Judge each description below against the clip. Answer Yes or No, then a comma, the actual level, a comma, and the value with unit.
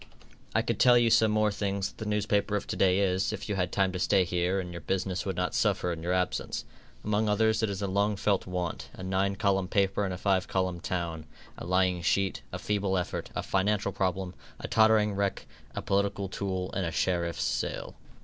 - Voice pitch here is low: Yes, very low, 95 Hz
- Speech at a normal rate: No, fast, 215 wpm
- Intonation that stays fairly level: Yes, narrow, 1.9 semitones